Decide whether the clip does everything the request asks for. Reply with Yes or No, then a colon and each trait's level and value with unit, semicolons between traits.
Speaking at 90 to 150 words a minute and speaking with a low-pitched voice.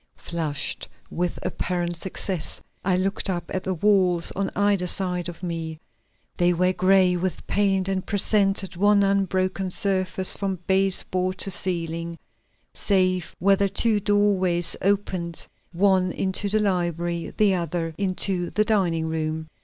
No: average, 140 wpm; medium, 185 Hz